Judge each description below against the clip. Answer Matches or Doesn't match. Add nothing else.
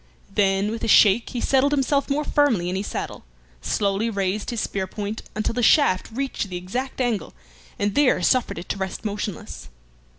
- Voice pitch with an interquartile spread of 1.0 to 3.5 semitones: Doesn't match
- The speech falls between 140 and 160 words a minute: Doesn't match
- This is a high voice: Matches